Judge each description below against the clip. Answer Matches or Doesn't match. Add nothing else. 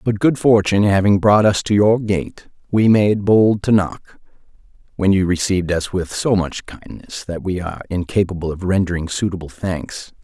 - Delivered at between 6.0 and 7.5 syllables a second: Doesn't match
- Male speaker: Matches